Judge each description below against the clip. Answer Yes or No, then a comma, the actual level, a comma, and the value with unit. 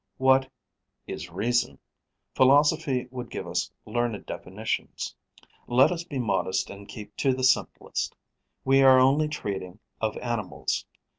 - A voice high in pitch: No, low, 125 Hz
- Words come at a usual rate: No, slow, 130 wpm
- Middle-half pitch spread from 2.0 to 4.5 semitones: Yes, average, 4.2 semitones